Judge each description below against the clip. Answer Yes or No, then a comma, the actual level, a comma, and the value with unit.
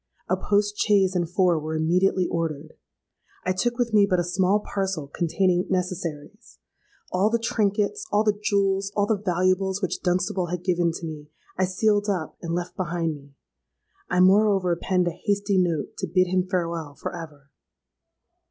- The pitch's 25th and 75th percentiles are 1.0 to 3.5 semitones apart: Yes, average, 2.8 semitones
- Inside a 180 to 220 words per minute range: No, average, 165 wpm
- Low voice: No, medium, 185 Hz